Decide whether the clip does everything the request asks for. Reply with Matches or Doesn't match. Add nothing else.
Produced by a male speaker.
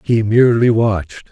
Matches